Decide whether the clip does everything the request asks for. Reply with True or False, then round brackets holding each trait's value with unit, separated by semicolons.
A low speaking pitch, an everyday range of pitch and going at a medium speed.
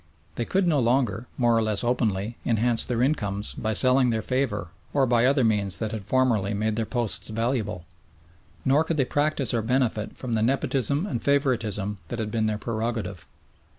True (115 Hz; 3.3 semitones; 185 wpm)